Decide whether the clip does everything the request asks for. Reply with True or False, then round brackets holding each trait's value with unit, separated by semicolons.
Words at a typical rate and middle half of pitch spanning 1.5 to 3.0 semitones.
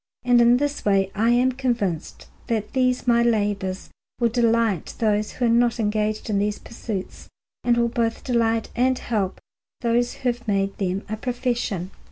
True (170 wpm; 2.7 semitones)